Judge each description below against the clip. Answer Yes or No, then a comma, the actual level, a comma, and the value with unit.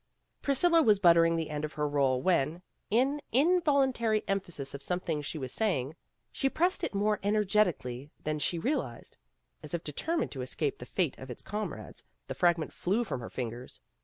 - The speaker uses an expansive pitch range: Yes, wide, 7.1 semitones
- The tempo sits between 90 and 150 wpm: No, average, 175 wpm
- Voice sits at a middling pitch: Yes, medium, 175 Hz